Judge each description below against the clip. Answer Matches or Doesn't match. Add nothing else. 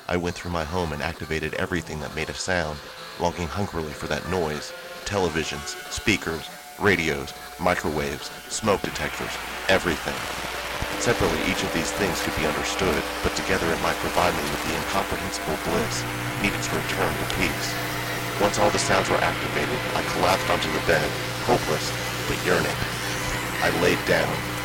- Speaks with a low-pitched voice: Matches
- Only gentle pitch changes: Doesn't match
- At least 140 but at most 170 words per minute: Matches